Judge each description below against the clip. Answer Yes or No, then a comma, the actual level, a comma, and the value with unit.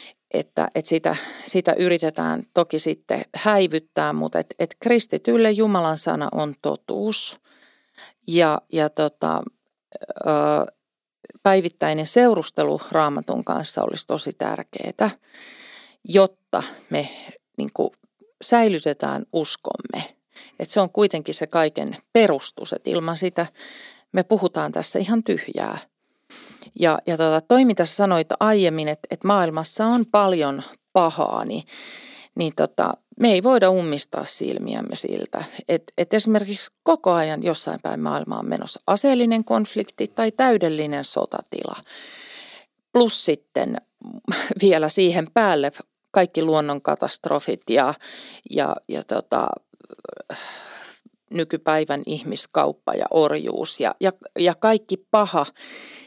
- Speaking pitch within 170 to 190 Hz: Yes, medium, 185 Hz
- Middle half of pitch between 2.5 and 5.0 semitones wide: No, wide, 5.6 semitones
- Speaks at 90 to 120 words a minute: Yes, average, 110 wpm